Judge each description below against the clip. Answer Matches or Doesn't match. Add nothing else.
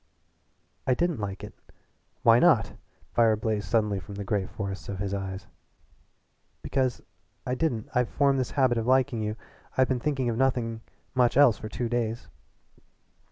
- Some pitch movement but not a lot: Matches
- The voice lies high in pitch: Doesn't match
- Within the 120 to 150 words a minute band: Doesn't match